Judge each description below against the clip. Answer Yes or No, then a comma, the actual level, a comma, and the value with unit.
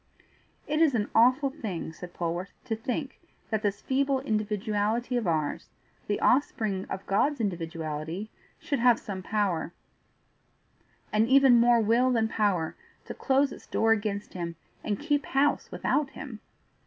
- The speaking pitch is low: No, high, 220 Hz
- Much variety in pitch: No, average, 5.0 semitones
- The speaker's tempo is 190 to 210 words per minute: No, average, 145 wpm